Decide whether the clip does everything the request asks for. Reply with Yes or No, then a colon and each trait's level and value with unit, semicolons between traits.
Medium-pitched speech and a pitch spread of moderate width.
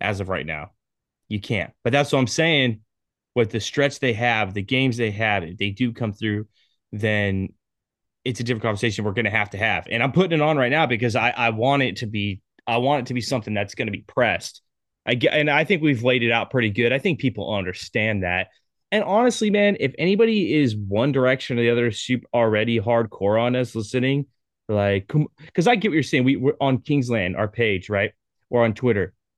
No: low, 120 Hz; average, 4.3 semitones